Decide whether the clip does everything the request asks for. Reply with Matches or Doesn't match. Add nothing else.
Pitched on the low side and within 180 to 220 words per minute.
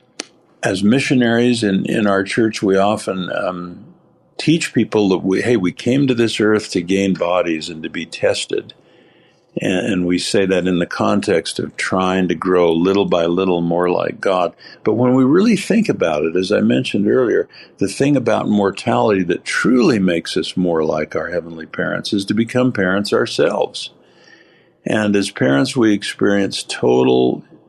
Doesn't match